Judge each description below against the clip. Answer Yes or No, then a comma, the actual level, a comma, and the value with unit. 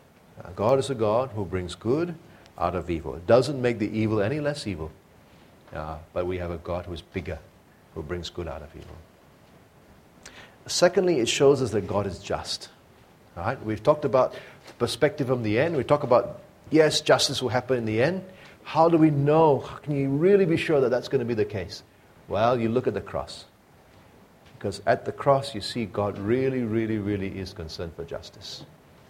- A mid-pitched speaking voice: No, low, 110 Hz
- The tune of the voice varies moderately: No, wide, 7.2 semitones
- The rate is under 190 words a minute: No, average, 195 wpm